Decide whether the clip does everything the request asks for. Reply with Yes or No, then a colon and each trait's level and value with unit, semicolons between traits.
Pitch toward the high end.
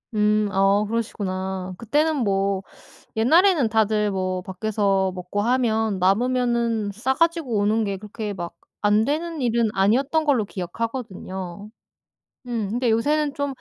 Yes: high, 215 Hz